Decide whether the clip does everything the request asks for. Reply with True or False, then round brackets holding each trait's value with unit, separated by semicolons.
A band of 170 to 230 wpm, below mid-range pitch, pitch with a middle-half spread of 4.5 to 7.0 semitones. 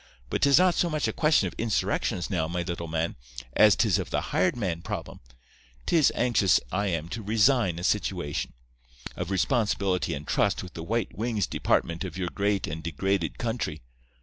True (180 wpm; 95 Hz; 5.0 semitones)